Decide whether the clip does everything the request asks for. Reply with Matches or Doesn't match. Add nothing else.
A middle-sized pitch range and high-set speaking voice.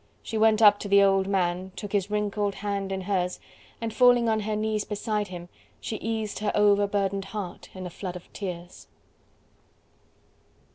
Doesn't match